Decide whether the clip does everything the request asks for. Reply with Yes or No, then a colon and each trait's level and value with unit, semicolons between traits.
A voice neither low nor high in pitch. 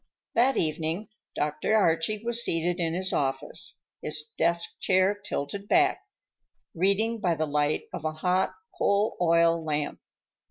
Yes: medium, 170 Hz